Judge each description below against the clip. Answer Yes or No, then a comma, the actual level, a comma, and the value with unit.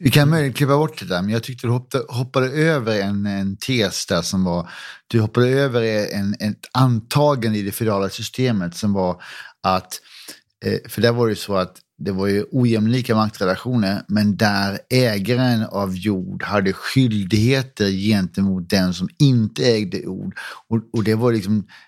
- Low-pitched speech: Yes, low, 110 Hz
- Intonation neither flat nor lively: Yes, average, 3.9 semitones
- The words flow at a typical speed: Yes, average, 175 wpm